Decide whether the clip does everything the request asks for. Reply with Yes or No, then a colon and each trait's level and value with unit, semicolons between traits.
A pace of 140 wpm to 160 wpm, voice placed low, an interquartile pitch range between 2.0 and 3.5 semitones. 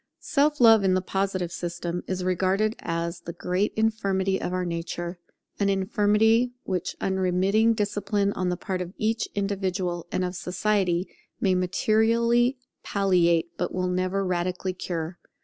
No: average, 145 wpm; high, 190 Hz; narrow, 2.5 semitones